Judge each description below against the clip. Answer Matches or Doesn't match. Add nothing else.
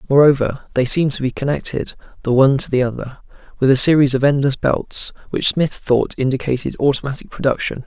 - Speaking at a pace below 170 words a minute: Doesn't match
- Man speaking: Matches